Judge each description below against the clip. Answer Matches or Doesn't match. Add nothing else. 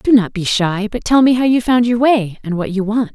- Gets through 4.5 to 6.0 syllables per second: Matches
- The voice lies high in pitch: Matches